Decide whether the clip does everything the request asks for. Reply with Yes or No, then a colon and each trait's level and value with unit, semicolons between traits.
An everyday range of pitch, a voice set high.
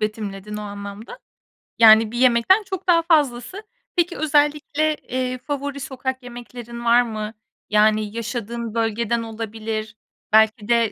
Yes: average, 3.9 semitones; high, 235 Hz